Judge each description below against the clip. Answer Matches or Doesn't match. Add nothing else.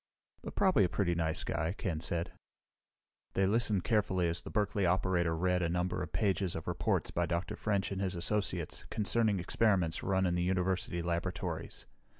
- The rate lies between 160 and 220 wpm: Matches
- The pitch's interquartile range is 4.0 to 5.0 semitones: Doesn't match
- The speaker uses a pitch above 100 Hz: Doesn't match